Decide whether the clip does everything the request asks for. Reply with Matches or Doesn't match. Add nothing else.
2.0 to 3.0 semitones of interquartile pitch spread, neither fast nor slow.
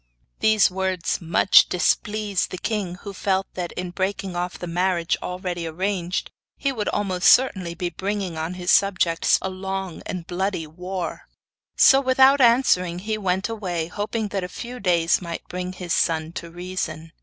Matches